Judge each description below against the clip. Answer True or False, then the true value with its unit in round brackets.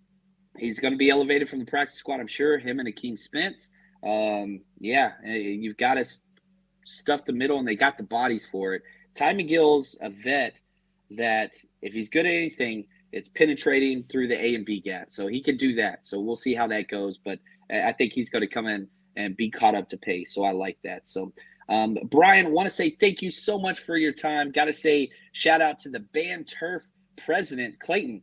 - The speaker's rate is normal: False (220 wpm)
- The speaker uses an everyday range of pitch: False (7.1 semitones)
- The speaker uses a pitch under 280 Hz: True (140 Hz)